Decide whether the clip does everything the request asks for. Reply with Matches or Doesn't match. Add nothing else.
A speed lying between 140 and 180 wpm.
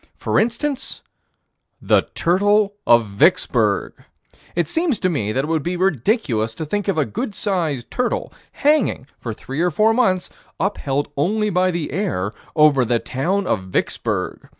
Matches